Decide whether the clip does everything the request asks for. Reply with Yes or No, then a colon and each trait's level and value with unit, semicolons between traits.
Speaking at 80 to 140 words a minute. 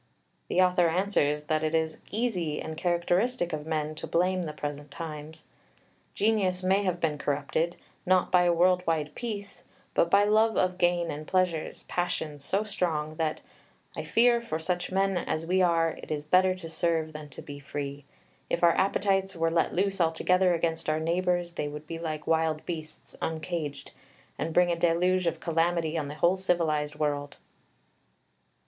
No: average, 175 wpm